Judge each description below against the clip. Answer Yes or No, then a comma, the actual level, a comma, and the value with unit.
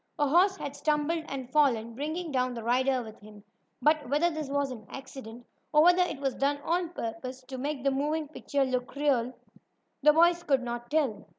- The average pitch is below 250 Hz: No, very high, 275 Hz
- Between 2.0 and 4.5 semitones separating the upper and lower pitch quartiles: Yes, average, 3.5 semitones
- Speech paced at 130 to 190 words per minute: No, average, 200 wpm